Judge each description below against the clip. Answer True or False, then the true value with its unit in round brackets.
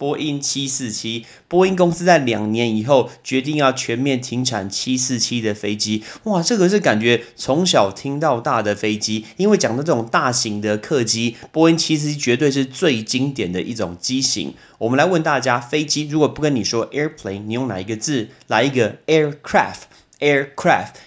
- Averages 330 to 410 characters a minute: True (350 characters per minute)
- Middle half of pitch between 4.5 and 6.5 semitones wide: True (5.1 semitones)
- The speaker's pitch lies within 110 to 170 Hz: True (130 Hz)